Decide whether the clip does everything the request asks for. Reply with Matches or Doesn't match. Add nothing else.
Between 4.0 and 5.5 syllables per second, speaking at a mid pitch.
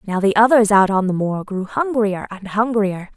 Doesn't match